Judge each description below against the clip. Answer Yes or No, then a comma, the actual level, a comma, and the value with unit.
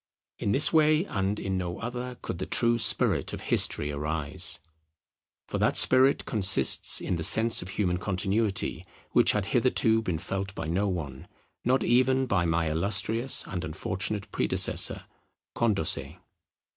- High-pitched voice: No, low, 100 Hz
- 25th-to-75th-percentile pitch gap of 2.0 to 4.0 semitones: No, average, 5.3 semitones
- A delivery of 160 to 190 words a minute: No, average, 145 wpm